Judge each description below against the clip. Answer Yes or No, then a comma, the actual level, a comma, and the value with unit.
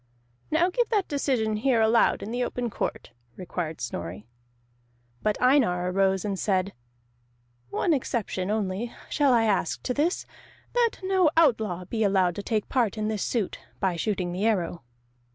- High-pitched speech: Yes, high, 215 Hz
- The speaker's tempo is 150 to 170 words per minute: Yes, average, 155 wpm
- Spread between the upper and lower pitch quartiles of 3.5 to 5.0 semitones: No, wide, 5.4 semitones